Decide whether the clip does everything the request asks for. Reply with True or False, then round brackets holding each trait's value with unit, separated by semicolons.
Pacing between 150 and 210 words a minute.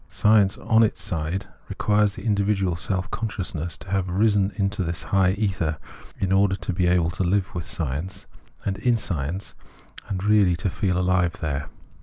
True (175 wpm)